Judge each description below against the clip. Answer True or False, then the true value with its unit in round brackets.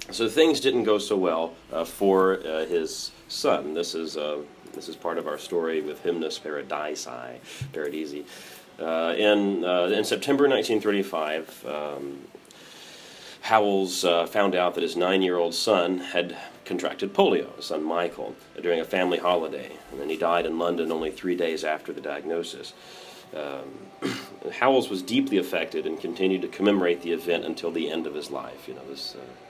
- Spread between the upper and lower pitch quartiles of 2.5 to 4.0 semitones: True (3.7 semitones)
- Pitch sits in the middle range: False (85 Hz)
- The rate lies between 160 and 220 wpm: True (165 wpm)